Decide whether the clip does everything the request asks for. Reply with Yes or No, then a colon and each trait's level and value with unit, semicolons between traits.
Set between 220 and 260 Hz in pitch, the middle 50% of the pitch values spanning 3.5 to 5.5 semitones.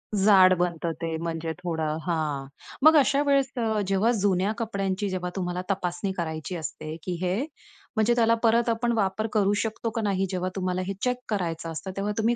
No: high, 190 Hz; average, 3.9 semitones